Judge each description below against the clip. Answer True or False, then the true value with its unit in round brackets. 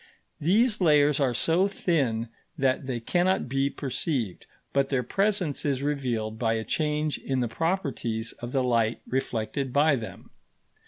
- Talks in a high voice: False (135 Hz)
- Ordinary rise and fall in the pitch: True (4.5 semitones)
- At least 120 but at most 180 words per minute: True (150 wpm)